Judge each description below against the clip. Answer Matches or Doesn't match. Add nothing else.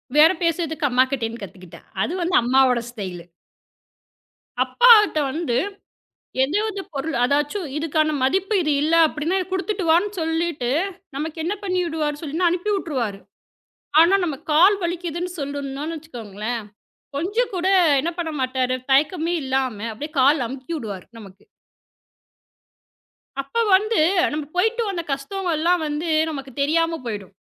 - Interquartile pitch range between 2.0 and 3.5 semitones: Doesn't match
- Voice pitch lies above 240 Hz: Matches